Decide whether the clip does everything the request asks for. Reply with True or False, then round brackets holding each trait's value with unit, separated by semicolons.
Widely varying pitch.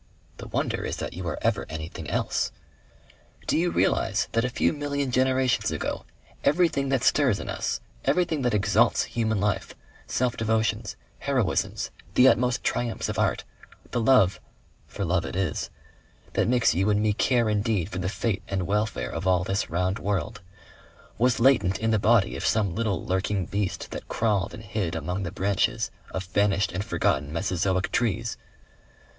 False (4.4 semitones)